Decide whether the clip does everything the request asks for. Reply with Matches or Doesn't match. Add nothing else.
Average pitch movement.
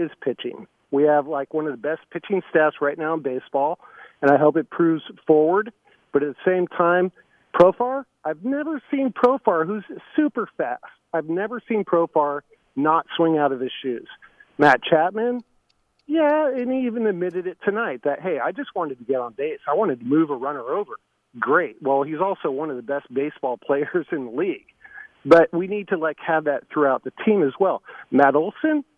Doesn't match